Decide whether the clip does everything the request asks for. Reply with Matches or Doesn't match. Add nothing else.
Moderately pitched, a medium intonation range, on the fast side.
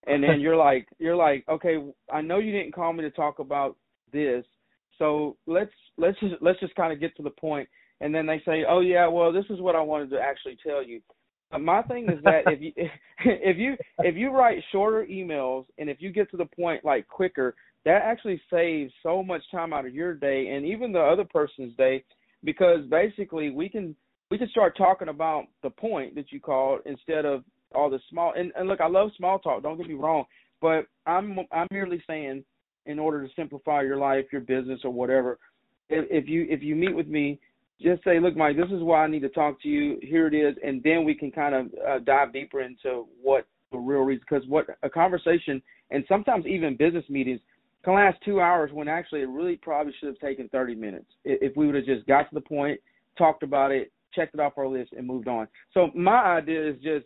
Matches